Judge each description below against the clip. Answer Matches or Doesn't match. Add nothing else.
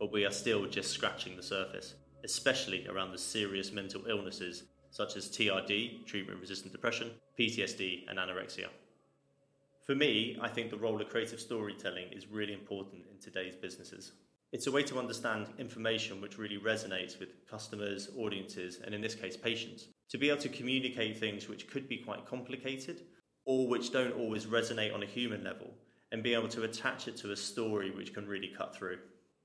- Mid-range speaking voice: Doesn't match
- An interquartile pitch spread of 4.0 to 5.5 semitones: Doesn't match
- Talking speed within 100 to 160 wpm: Doesn't match